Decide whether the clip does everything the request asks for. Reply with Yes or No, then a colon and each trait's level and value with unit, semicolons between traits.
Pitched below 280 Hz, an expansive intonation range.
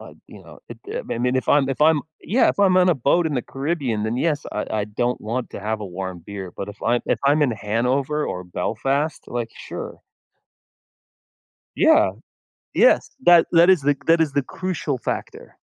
Yes: low, 135 Hz; wide, 6.5 semitones